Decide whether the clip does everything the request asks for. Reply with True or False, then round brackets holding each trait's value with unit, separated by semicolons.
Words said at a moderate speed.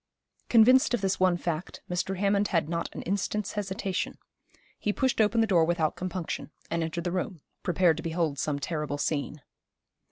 True (170 wpm)